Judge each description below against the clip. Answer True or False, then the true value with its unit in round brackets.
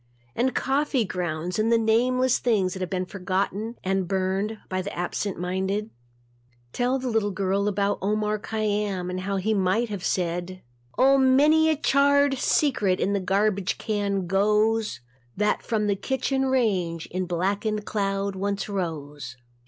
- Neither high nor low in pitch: False (200 Hz)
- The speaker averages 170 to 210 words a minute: False (150 wpm)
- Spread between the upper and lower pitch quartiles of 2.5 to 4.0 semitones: True (3.3 semitones)